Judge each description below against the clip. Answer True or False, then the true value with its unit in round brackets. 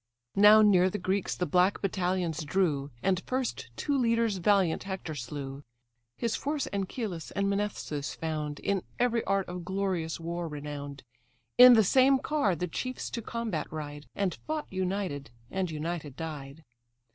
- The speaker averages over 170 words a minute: False (150 wpm)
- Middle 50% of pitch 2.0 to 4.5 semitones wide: False (4.9 semitones)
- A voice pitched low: False (185 Hz)